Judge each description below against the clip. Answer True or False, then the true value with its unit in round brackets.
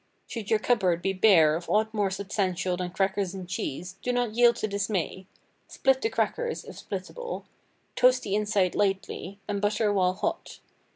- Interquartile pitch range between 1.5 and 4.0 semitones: True (2.9 semitones)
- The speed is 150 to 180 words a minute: True (170 wpm)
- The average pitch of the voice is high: True (200 Hz)